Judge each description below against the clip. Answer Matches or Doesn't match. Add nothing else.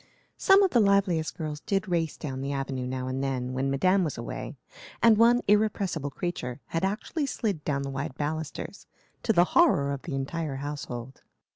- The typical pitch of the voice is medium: Matches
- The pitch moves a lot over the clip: Matches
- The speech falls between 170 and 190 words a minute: Matches